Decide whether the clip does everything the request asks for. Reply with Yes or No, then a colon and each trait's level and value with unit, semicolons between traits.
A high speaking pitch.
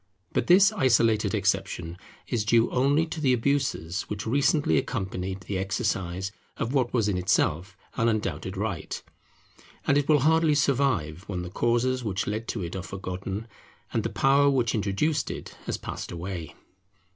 No: low, 110 Hz